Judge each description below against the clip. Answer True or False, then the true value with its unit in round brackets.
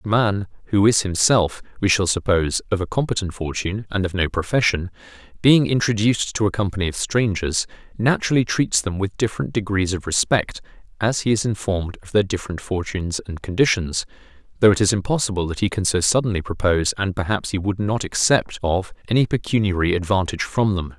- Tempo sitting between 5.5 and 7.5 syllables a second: True (5.9 syllables/s)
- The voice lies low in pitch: True (100 Hz)